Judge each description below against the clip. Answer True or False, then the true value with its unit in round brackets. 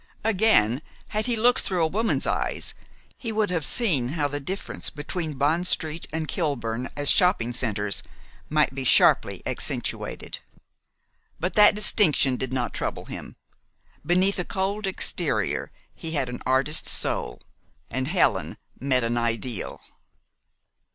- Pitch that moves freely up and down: True (6.6 semitones)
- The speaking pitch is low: False (155 Hz)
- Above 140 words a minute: False (135 wpm)